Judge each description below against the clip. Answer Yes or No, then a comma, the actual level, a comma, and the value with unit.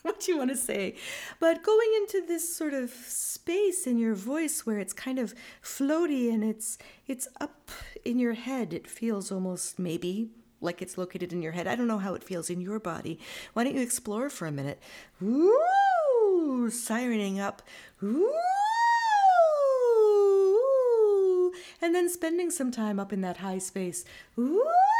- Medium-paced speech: Yes, average, 165 wpm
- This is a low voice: No, very high, 260 Hz